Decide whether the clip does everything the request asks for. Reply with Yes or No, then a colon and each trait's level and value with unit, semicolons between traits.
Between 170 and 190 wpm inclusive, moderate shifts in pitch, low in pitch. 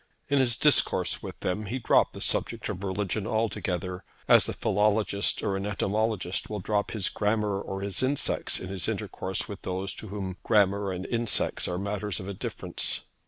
No: average, 175 wpm; narrow, 2.1 semitones; low, 100 Hz